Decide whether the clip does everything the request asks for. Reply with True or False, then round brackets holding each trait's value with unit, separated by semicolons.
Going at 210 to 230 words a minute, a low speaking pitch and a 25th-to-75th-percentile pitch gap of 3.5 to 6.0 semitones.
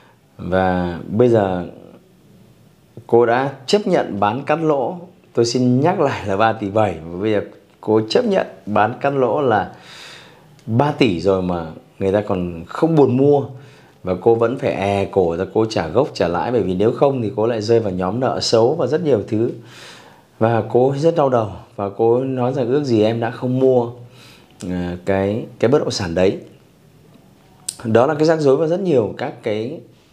False (195 wpm; 115 Hz; 5.3 semitones)